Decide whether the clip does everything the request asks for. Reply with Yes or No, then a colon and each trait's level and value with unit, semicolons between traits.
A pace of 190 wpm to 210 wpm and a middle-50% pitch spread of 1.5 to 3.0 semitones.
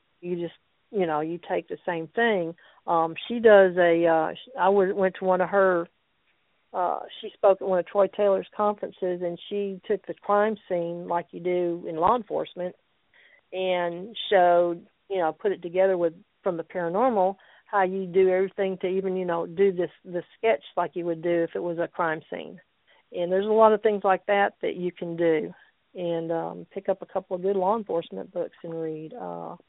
Yes: average, 200 wpm; narrow, 2.4 semitones